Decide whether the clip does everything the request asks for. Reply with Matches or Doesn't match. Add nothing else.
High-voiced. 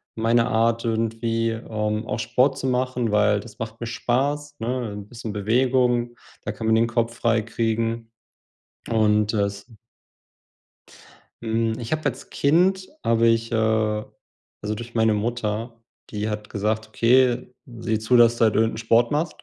Doesn't match